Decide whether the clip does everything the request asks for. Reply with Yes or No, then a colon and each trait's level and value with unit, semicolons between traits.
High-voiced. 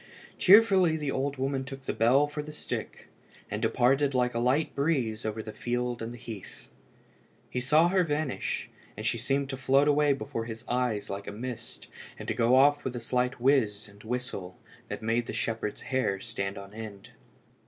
No: low, 125 Hz